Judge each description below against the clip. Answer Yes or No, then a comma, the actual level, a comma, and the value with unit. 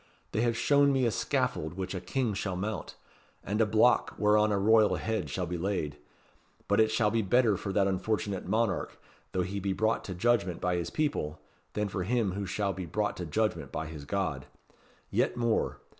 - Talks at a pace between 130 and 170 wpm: No, average, 200 wpm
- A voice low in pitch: Yes, low, 100 Hz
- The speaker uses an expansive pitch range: No, average, 3.4 semitones